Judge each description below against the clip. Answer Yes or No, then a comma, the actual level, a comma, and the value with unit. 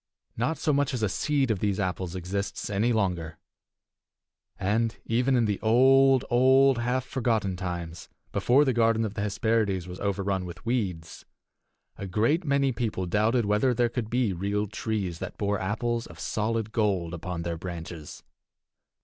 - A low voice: Yes, low, 105 Hz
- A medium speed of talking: Yes, average, 160 wpm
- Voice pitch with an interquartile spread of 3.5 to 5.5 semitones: Yes, average, 4.4 semitones